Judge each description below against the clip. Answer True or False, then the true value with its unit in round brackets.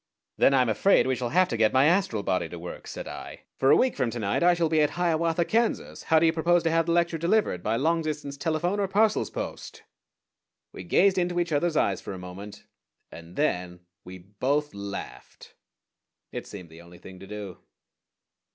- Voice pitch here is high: False (150 Hz)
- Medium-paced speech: False (215 wpm)